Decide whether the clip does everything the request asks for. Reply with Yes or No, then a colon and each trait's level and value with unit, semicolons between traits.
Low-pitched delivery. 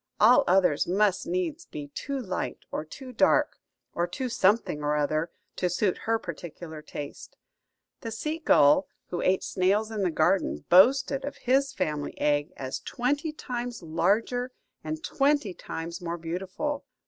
No: high, 190 Hz